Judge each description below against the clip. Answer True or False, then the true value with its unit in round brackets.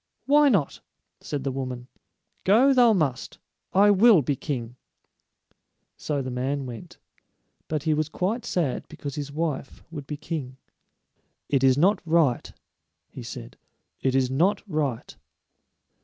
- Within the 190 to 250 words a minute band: False (140 wpm)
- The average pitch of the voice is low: False (150 Hz)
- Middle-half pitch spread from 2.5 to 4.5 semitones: False (5.5 semitones)